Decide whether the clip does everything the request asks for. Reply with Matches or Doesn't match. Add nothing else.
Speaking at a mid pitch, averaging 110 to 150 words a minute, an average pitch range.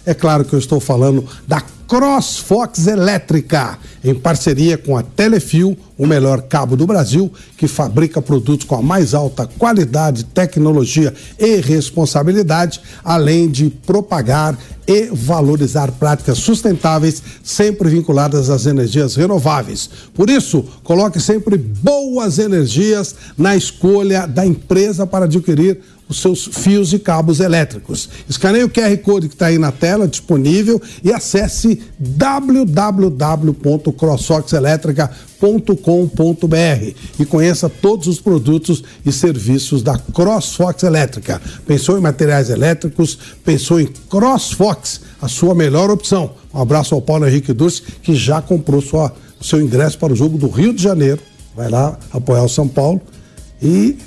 Matches